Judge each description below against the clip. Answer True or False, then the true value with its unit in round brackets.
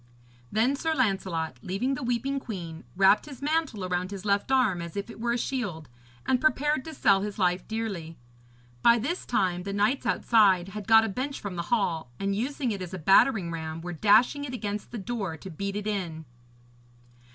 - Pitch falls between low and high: False (205 Hz)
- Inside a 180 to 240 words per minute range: True (195 wpm)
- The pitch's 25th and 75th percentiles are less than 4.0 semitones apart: False (5.2 semitones)